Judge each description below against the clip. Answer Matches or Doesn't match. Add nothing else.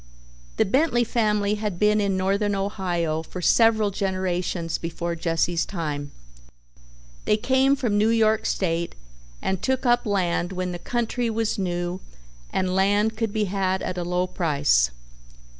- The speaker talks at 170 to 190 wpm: Doesn't match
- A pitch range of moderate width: Matches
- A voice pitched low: Doesn't match